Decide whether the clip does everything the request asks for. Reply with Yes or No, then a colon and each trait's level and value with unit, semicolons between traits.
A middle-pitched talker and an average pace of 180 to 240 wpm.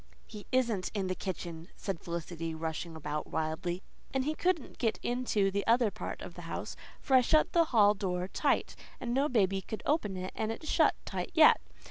No: high, 200 Hz; average, 195 wpm